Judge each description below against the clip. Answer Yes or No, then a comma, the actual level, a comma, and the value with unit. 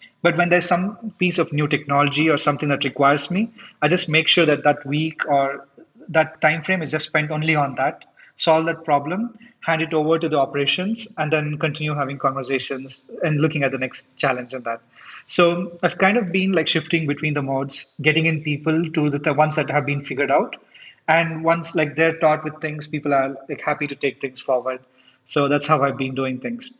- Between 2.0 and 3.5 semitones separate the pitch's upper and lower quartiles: Yes, average, 2.7 semitones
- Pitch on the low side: No, medium, 155 Hz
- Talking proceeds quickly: Yes, fast, 215 wpm